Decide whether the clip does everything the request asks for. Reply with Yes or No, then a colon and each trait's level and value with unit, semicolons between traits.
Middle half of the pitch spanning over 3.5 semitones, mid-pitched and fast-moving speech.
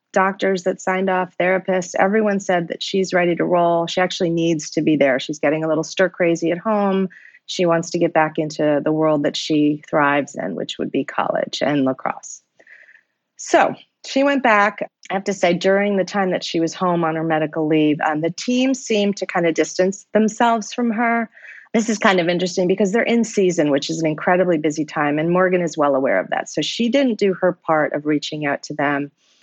Yes: average, 3.9 semitones; medium, 180 Hz; fast, 220 wpm